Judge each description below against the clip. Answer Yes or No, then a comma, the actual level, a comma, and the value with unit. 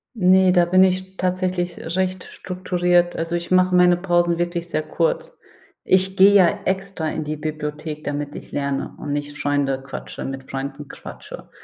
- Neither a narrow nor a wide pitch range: Yes, average, 3.7 semitones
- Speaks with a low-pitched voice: No, medium, 175 Hz